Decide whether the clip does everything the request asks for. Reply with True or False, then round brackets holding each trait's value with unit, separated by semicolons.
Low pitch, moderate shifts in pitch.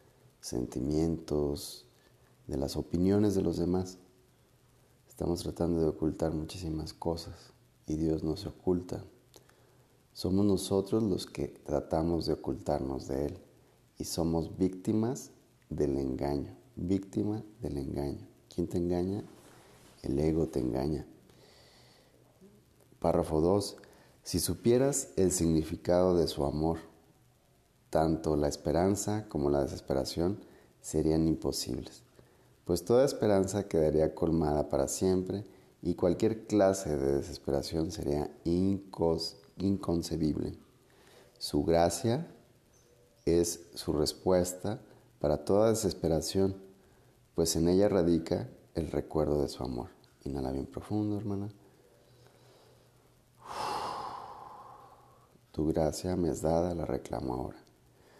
True (85 Hz; 4.5 semitones)